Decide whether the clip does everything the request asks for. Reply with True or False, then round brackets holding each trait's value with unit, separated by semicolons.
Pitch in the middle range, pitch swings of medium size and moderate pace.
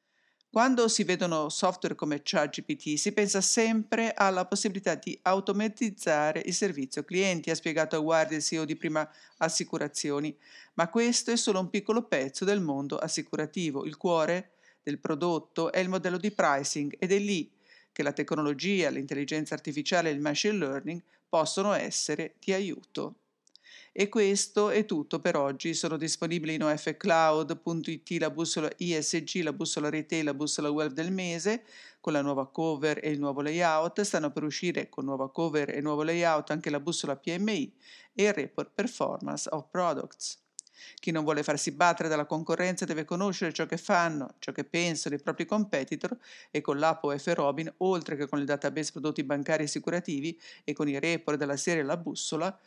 True (165 Hz; 3.7 semitones; 170 wpm)